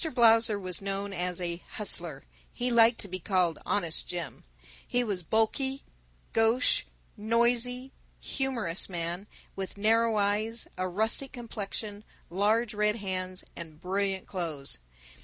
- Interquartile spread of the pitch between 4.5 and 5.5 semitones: No, average, 3.9 semitones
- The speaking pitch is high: Yes, high, 205 Hz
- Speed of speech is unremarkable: No, slow, 130 wpm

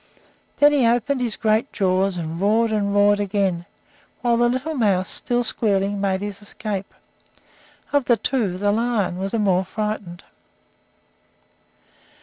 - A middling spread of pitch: Yes, average, 3.4 semitones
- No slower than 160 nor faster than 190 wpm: No, average, 140 wpm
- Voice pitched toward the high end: Yes, high, 205 Hz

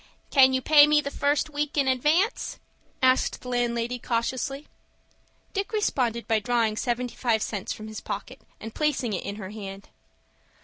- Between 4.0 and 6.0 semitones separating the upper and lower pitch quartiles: Yes, average, 4.4 semitones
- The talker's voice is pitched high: Yes, very high, 250 Hz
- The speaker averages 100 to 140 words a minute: No, average, 165 wpm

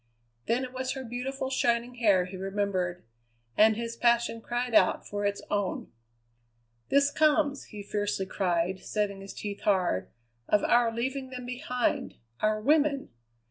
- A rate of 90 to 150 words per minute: Yes, average, 145 wpm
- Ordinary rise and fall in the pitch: Yes, average, 4.1 semitones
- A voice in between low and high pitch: No, high, 230 Hz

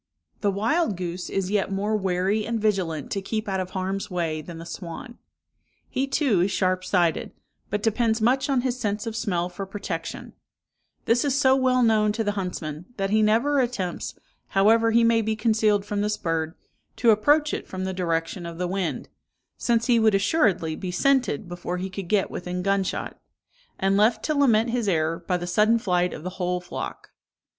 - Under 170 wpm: No, average, 195 wpm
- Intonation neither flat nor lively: Yes, average, 4.0 semitones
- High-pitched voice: Yes, high, 200 Hz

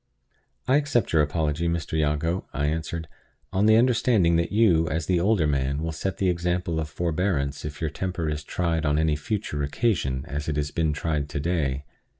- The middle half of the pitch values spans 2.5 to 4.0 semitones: Yes, average, 3.3 semitones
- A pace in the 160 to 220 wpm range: Yes, average, 185 wpm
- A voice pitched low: Yes, very low, 80 Hz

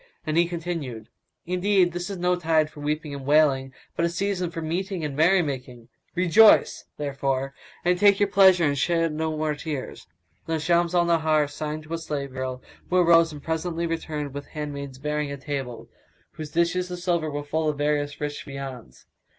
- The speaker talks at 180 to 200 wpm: Yes, average, 185 wpm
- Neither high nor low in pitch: Yes, medium, 155 Hz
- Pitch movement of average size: Yes, average, 3.2 semitones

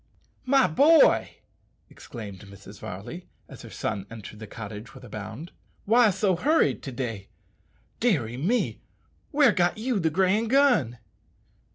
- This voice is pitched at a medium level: Yes, medium, 165 Hz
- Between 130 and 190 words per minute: Yes, average, 140 wpm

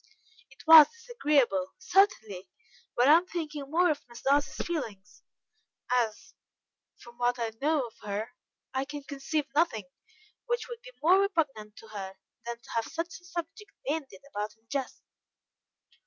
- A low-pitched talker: No, very high, 280 Hz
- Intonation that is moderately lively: No, wide, 6.8 semitones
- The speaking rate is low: No, average, 155 wpm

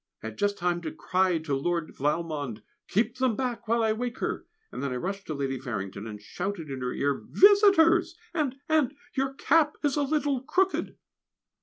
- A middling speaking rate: Yes, average, 190 wpm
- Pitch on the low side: No, high, 200 Hz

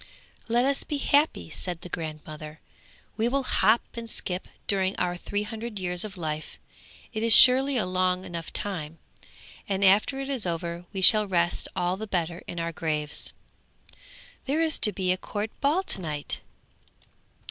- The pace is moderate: Yes, average, 170 wpm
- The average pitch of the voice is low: No, high, 190 Hz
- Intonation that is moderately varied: Yes, average, 5.0 semitones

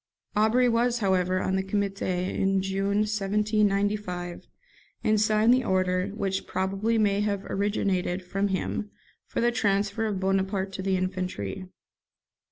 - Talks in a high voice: Yes, high, 195 Hz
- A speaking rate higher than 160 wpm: No, slow, 135 wpm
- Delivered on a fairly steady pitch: Yes, narrow, 2.0 semitones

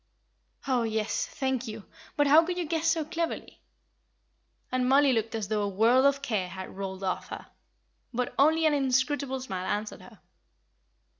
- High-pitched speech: Yes, very high, 255 Hz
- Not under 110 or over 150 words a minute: No, average, 165 wpm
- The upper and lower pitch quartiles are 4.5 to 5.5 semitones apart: Yes, average, 5.2 semitones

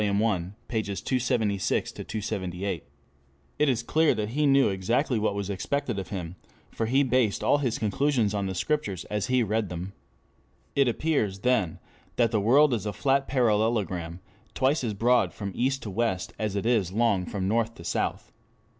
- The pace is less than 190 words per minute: Yes, average, 170 wpm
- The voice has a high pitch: No, low, 110 Hz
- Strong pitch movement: No, average, 4.3 semitones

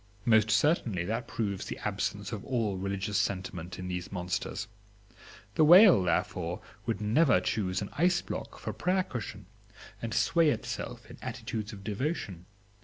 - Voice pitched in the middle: No, low, 105 Hz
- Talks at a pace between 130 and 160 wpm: Yes, average, 150 wpm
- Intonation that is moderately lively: Yes, average, 4.8 semitones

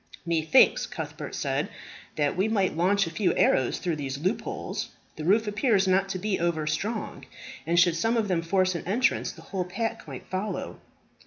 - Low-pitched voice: No, medium, 185 Hz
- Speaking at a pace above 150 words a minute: Yes, average, 180 wpm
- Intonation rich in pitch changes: No, average, 3.7 semitones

